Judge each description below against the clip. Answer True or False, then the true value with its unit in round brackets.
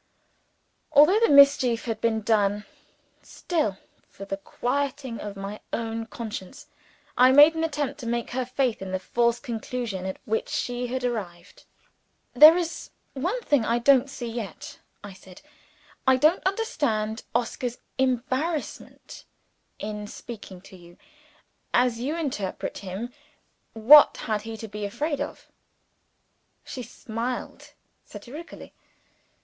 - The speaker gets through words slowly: True (130 wpm)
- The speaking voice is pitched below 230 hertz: False (240 Hz)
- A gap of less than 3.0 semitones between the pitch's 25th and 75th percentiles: False (4.7 semitones)